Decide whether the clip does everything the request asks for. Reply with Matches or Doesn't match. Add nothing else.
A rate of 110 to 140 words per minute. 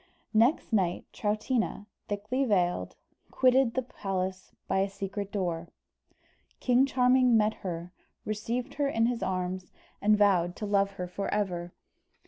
Matches